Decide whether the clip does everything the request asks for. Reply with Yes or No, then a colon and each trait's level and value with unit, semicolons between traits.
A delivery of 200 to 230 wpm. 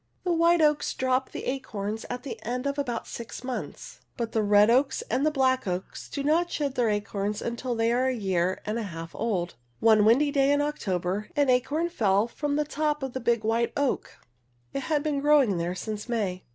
Yes: fast, 205 wpm